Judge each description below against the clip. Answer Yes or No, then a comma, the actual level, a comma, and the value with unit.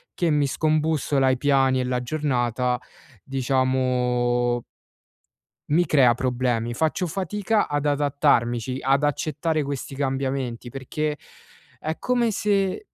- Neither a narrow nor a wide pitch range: Yes, average, 3.5 semitones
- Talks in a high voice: No, low, 135 Hz